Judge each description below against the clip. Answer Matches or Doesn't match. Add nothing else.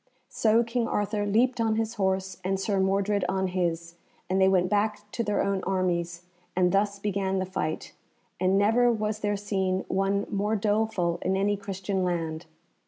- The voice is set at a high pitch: Matches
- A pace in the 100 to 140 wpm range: Doesn't match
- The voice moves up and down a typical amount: Doesn't match